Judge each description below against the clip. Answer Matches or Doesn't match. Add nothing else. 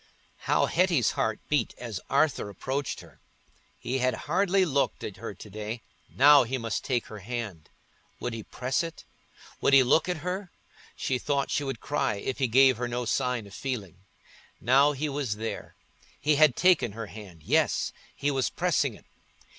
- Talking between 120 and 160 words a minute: Doesn't match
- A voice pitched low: Matches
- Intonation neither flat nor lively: Matches